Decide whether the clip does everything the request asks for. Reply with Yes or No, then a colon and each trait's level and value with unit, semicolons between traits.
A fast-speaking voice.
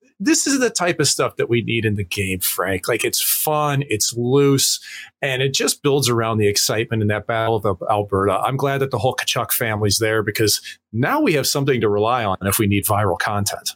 Yes: fast, 220 wpm